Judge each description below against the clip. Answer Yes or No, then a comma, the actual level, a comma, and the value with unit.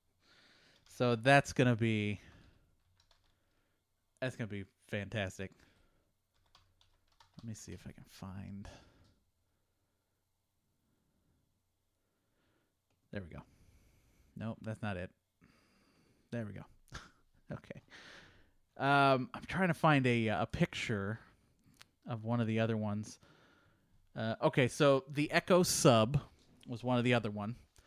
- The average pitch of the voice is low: Yes, low, 110 Hz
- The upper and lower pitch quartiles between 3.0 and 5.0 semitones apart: Yes, average, 4.1 semitones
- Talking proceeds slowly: Yes, slow, 110 wpm